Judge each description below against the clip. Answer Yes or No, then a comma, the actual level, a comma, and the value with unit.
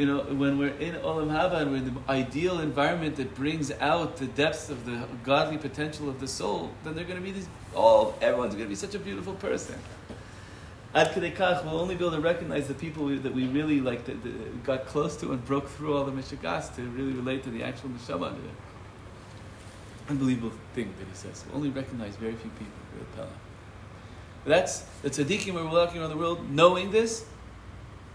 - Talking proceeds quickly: Yes, fast, 215 wpm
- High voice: No, low, 135 Hz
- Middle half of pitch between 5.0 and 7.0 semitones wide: Yes, wide, 5.4 semitones